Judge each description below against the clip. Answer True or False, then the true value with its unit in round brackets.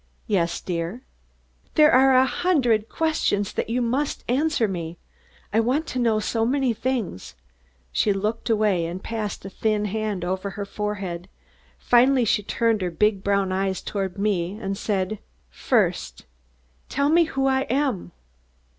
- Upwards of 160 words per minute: False (155 wpm)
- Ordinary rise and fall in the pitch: True (4.7 semitones)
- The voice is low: False (215 Hz)